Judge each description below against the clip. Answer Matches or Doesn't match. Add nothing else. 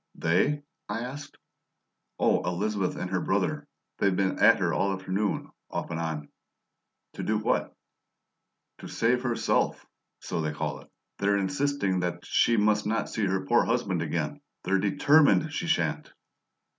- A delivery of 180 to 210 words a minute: Doesn't match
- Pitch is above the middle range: Doesn't match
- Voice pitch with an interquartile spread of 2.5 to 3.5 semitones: Doesn't match